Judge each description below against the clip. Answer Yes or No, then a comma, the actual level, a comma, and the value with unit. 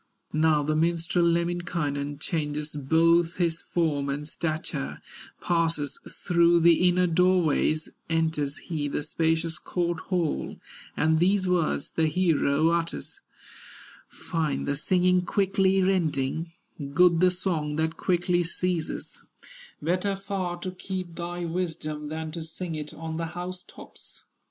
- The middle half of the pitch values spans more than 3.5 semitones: No, narrow, 2.4 semitones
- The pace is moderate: No, slow, 130 wpm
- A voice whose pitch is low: No, medium, 165 Hz